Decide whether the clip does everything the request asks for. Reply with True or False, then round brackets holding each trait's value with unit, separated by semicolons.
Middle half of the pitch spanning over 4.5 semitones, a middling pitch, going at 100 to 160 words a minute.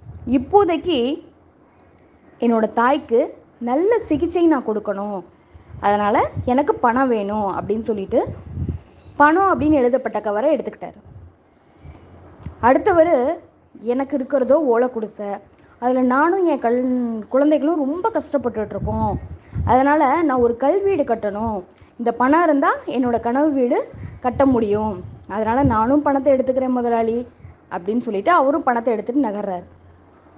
False (5.4 semitones; 245 Hz; 105 wpm)